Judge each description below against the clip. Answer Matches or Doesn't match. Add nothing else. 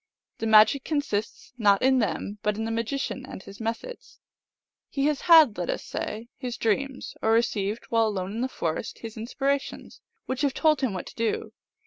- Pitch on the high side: Matches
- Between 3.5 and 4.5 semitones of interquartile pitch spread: Matches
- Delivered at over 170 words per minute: Matches